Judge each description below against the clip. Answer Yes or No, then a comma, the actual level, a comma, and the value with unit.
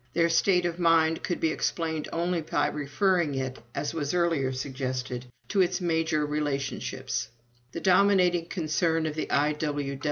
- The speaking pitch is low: No, medium, 160 Hz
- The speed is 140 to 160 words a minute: Yes, average, 150 wpm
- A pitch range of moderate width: Yes, average, 3.1 semitones